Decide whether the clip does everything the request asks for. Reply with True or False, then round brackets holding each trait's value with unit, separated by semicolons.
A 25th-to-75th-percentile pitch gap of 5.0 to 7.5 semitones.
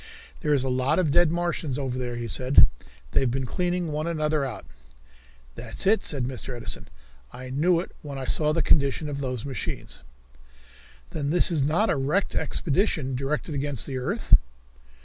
False (3.7 semitones)